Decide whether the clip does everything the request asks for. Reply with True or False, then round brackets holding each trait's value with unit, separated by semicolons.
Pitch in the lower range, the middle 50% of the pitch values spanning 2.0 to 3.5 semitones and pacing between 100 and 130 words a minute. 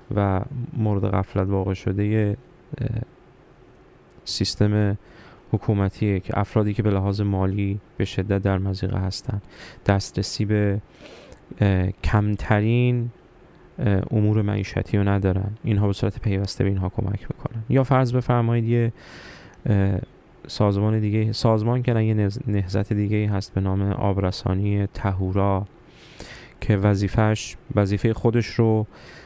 True (105 Hz; 2.4 semitones; 110 wpm)